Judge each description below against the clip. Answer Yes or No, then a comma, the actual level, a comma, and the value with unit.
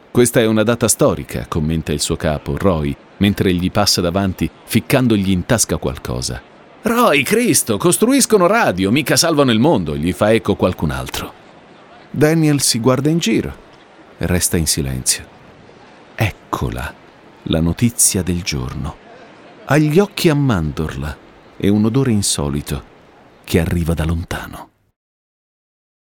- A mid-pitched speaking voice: No, very low, 95 Hz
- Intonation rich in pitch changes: Yes, wide, 7.0 semitones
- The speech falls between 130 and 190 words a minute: Yes, average, 135 wpm